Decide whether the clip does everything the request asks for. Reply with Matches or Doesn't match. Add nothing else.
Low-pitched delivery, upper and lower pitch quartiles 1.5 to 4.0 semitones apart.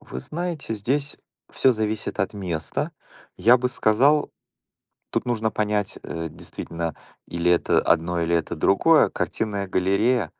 Doesn't match